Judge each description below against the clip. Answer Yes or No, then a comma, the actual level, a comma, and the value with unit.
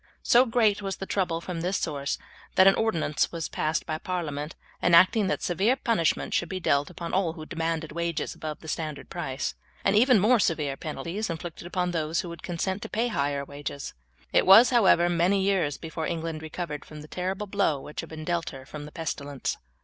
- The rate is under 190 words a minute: No, average, 200 wpm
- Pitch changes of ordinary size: Yes, average, 3.7 semitones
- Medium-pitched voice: Yes, medium, 170 Hz